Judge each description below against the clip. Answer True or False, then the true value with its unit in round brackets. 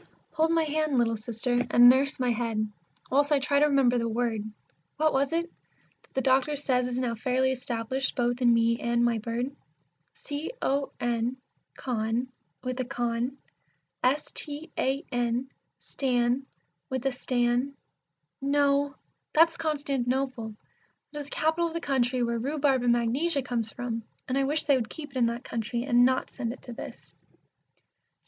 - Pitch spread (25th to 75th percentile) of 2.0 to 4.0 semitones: True (2.8 semitones)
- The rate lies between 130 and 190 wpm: True (170 wpm)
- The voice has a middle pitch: False (255 Hz)